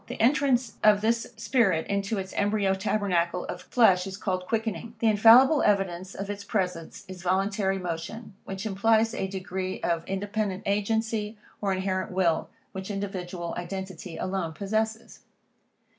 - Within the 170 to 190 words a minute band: No, average, 145 wpm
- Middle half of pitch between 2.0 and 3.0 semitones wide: Yes, average, 2.7 semitones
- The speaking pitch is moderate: No, high, 195 Hz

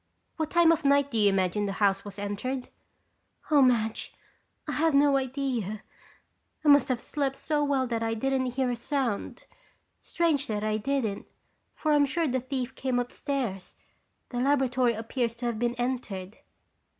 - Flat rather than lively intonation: No, average, 4.0 semitones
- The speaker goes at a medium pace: Yes, average, 165 wpm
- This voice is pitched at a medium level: No, very high, 255 Hz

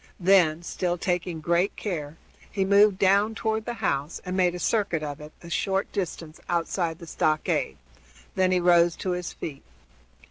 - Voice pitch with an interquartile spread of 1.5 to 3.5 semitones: Yes, average, 2.9 semitones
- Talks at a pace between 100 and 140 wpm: No, average, 170 wpm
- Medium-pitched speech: Yes, medium, 175 Hz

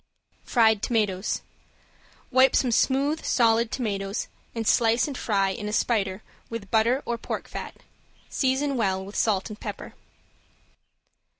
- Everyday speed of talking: No, slow, 130 wpm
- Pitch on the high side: Yes, high, 225 Hz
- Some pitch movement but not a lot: Yes, average, 3.5 semitones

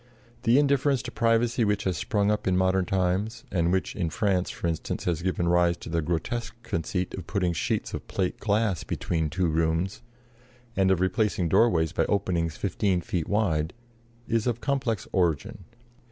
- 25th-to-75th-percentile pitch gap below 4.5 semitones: Yes, average, 4.0 semitones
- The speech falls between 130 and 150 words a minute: No, average, 170 wpm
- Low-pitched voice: Yes, very low, 95 Hz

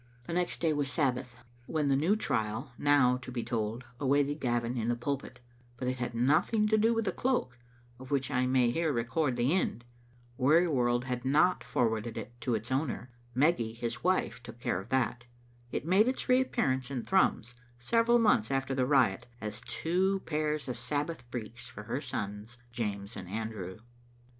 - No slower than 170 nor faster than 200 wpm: Yes, average, 180 wpm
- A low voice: Yes, low, 125 Hz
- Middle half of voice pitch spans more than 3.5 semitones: Yes, average, 4.2 semitones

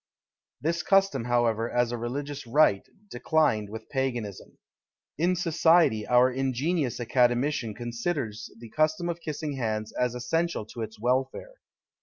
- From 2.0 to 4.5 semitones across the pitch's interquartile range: No, average, 5.0 semitones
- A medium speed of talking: No, slow, 130 wpm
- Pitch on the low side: Yes, low, 125 Hz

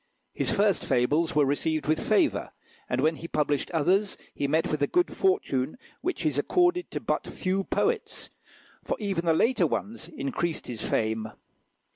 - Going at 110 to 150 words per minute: No, average, 165 wpm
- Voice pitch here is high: No, medium, 160 Hz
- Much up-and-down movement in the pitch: Yes, wide, 6.0 semitones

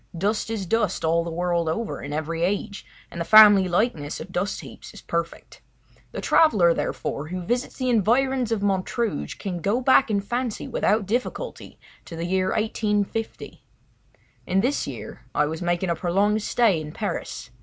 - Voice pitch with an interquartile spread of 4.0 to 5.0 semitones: Yes, average, 4.6 semitones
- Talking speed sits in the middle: Yes, average, 175 wpm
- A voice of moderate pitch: No, high, 200 Hz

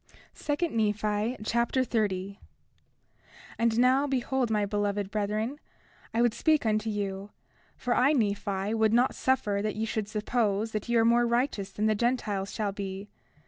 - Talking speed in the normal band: Yes, average, 160 wpm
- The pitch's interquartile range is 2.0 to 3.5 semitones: Yes, average, 2.7 semitones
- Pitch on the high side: Yes, high, 220 Hz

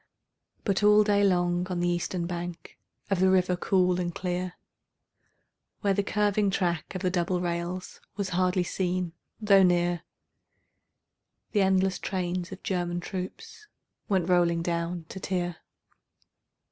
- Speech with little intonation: Yes, narrow, 1.5 semitones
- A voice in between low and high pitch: Yes, medium, 180 Hz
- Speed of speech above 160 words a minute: No, slow, 135 wpm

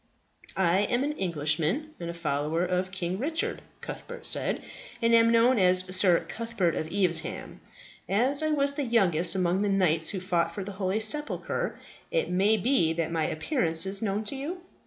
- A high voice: Yes, high, 195 Hz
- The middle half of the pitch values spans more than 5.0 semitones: Yes, wide, 5.6 semitones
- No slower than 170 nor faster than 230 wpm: Yes, average, 180 wpm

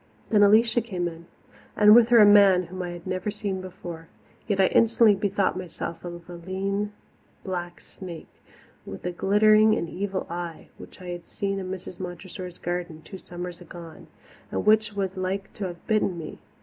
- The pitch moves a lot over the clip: No, average, 2.7 semitones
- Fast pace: No, average, 180 wpm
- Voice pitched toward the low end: No, medium, 185 Hz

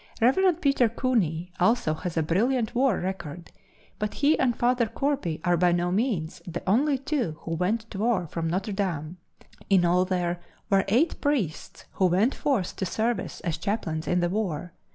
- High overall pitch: Yes, high, 195 Hz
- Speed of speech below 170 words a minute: No, average, 175 wpm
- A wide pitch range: Yes, wide, 5.7 semitones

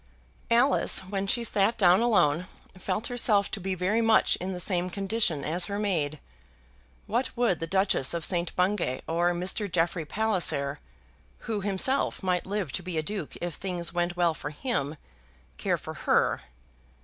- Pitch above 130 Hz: Yes, medium, 185 Hz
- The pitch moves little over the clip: No, average, 3.4 semitones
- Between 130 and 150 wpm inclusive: No, average, 165 wpm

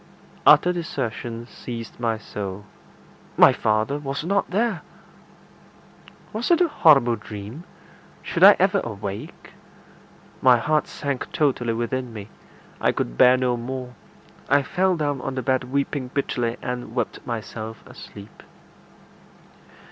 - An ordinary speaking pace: No, slow, 125 wpm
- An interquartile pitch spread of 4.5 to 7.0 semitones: No, average, 4.0 semitones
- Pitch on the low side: Yes, low, 125 Hz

